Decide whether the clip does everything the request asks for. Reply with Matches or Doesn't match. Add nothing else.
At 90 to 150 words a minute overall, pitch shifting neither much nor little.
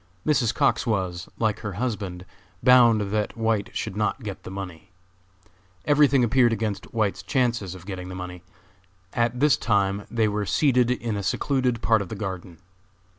Doesn't match